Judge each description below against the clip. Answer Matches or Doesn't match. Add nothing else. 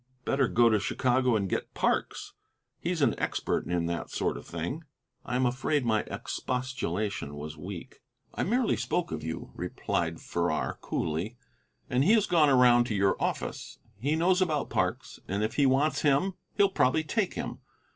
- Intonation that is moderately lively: Doesn't match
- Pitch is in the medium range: Doesn't match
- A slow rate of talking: Doesn't match